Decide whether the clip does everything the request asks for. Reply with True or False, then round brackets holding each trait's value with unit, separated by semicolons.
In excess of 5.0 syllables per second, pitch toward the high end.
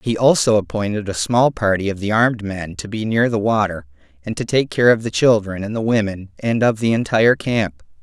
False (5.5 syllables/s; 105 Hz)